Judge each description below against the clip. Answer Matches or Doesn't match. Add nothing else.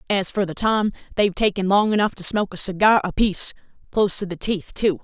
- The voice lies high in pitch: Matches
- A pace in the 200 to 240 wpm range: Matches